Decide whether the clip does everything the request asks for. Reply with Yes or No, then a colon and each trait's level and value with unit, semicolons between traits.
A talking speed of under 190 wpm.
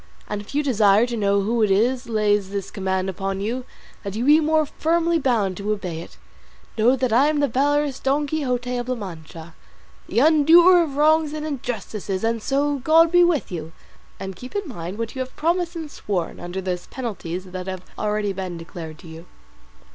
No: average, 200 wpm